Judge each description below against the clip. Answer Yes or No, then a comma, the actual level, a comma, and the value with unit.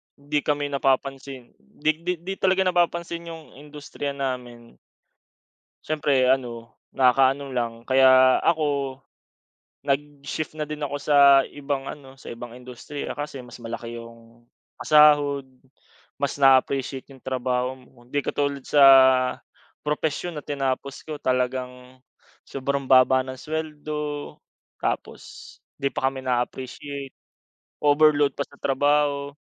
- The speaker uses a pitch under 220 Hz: Yes, medium, 140 Hz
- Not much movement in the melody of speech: Yes, narrow, 2.2 semitones